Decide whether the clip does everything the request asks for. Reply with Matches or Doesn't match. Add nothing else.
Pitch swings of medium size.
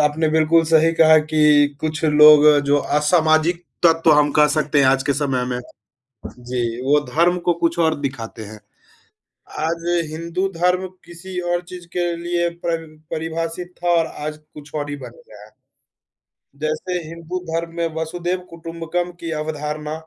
Doesn't match